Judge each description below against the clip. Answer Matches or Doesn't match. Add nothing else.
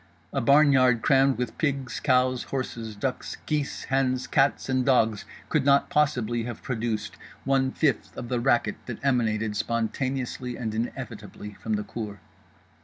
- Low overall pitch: Matches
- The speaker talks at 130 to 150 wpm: Matches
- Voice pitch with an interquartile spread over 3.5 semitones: Doesn't match